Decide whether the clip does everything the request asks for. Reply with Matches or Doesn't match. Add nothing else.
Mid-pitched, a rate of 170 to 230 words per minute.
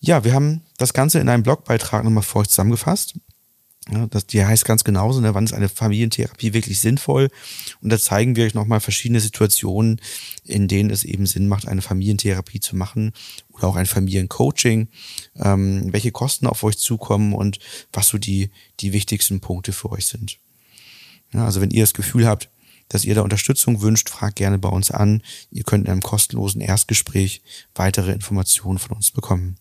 Doesn't match